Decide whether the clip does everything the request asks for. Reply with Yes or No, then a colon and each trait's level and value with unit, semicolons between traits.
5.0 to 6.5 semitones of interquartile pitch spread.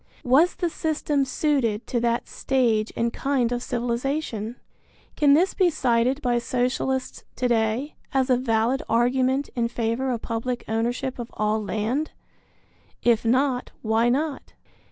No: narrow, 2.6 semitones